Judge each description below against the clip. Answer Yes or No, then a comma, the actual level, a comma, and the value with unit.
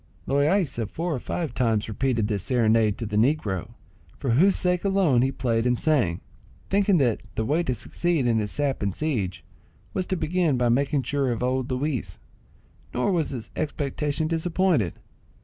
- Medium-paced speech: Yes, average, 170 wpm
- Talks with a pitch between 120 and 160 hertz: Yes, low, 135 Hz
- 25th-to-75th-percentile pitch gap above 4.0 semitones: Yes, wide, 5.6 semitones